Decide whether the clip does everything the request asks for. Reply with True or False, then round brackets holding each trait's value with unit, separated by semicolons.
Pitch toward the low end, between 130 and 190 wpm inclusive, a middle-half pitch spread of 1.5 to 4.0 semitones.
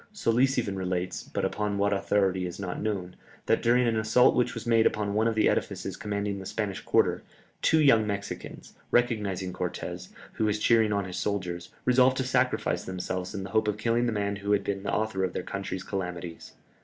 False (100 Hz; 205 wpm; 3.0 semitones)